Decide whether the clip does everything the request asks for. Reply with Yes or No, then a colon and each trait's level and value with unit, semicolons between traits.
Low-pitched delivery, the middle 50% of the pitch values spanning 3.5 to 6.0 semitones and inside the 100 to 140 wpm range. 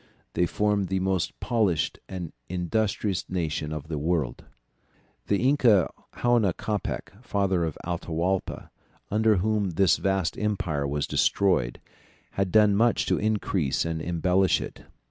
Yes: very low, 95 Hz; average, 3.9 semitones; slow, 135 wpm